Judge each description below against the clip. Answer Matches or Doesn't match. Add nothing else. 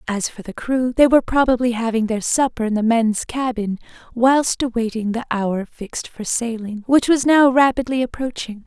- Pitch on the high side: Matches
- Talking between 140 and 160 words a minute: Doesn't match